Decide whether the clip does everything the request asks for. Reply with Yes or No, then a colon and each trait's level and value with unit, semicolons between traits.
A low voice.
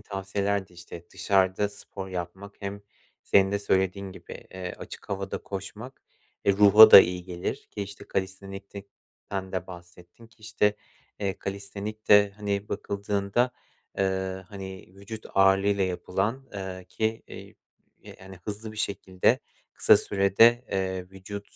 Yes: low, 100 Hz